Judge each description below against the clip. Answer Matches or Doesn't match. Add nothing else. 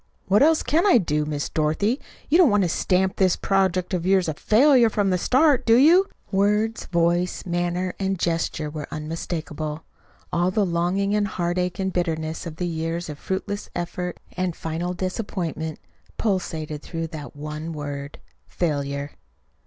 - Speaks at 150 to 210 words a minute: Matches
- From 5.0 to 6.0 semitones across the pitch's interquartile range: Doesn't match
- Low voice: Doesn't match